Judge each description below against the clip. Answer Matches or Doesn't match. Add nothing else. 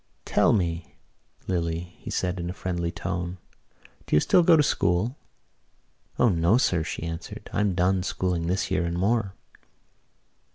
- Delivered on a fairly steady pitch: Matches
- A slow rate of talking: Doesn't match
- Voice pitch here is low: Matches